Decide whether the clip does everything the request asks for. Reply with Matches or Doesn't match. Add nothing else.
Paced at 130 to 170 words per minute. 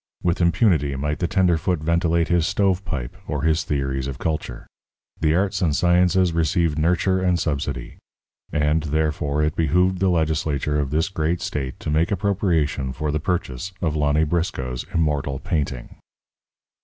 Matches